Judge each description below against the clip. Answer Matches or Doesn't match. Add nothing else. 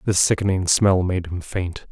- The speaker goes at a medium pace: Matches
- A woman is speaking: Doesn't match